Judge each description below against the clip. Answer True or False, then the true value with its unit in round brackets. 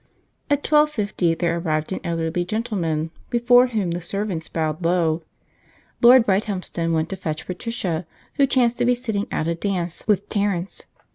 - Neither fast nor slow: True (160 wpm)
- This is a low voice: False (185 Hz)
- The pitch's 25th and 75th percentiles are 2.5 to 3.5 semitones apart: False (5.5 semitones)